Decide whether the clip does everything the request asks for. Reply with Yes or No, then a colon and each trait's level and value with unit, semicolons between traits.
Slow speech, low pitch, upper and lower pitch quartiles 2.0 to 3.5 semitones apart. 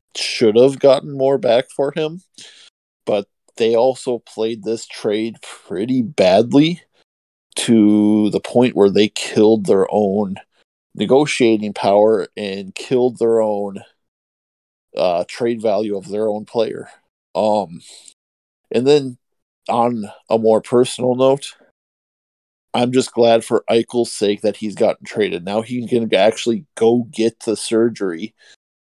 Yes: slow, 130 wpm; low, 115 Hz; average, 2.8 semitones